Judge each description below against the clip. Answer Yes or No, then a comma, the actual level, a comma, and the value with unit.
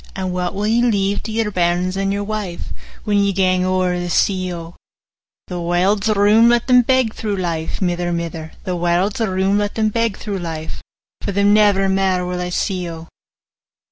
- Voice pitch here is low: No, high, 190 Hz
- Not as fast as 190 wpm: No, average, 195 wpm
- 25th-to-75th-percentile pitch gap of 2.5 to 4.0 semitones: Yes, average, 2.8 semitones